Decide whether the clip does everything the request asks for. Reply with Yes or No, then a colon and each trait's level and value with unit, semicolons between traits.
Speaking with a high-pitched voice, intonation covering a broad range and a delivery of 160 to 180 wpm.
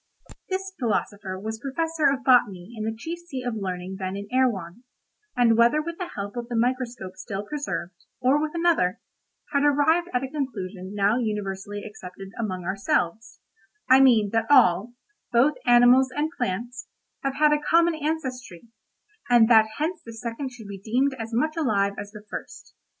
Yes: high, 240 Hz; wide, 5.7 semitones; average, 165 wpm